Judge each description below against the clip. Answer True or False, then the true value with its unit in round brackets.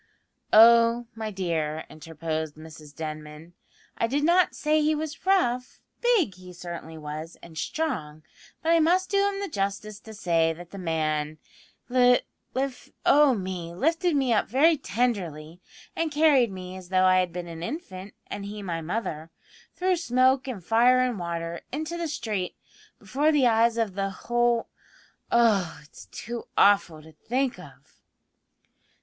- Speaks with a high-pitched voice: True (210 Hz)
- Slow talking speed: False (155 wpm)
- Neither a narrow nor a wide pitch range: False (7.9 semitones)